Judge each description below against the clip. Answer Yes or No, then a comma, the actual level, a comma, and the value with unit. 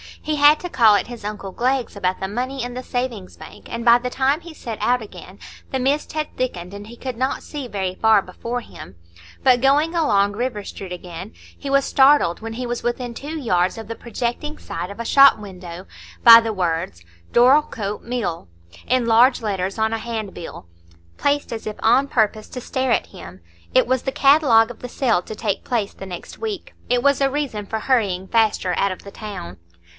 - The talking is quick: Yes, fast, 210 wpm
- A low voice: No, high, 230 Hz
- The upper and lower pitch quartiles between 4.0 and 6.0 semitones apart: Yes, average, 4.5 semitones